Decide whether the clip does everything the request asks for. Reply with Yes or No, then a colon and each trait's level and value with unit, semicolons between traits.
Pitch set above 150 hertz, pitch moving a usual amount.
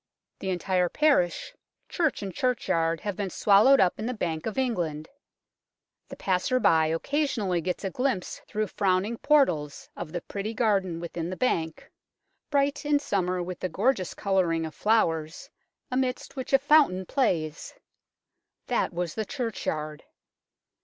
No: high, 190 Hz; wide, 6.7 semitones